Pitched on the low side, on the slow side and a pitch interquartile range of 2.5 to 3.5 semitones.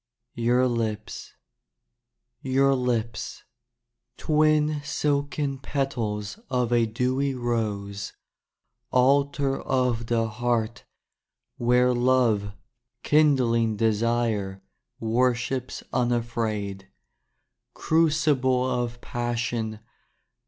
Yes: low, 120 Hz; slow, 70 wpm; average, 2.9 semitones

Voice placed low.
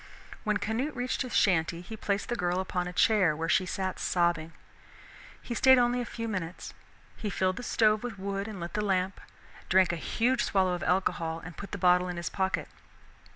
No: high, 190 Hz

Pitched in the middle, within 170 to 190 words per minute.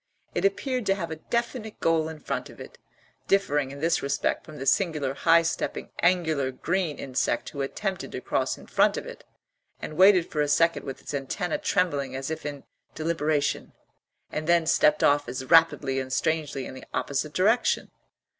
Yes: medium, 155 Hz; average, 185 wpm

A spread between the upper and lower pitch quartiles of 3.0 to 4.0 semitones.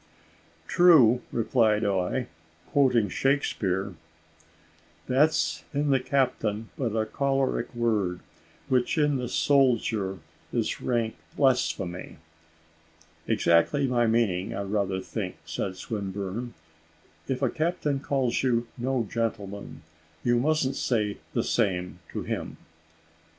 No: average, 4.8 semitones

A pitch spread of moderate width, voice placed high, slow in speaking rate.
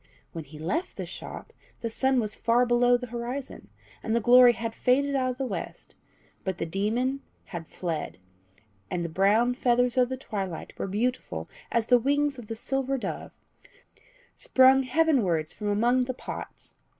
No: average, 3.8 semitones; high, 245 Hz; average, 170 wpm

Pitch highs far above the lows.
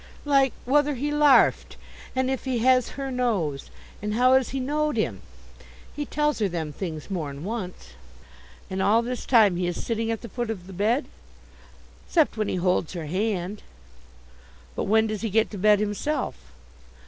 Yes: wide, 5.7 semitones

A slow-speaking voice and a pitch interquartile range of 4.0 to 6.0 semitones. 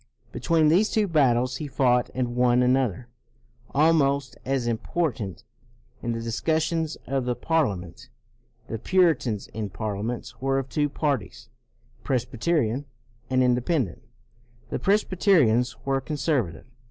Yes: slow, 115 wpm; average, 4.5 semitones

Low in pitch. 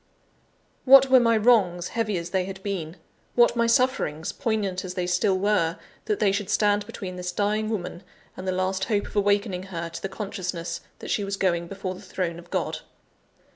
No: high, 195 Hz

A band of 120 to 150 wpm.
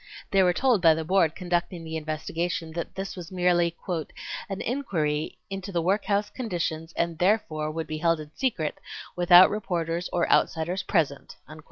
No: average, 160 wpm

